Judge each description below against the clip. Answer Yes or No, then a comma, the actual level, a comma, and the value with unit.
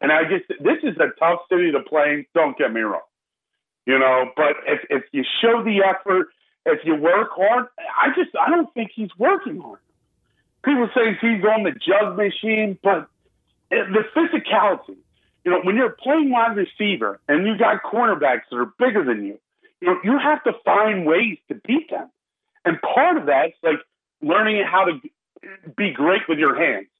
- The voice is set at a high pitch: Yes, high, 220 Hz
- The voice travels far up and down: Yes, wide, 7.8 semitones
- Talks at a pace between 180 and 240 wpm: Yes, average, 190 wpm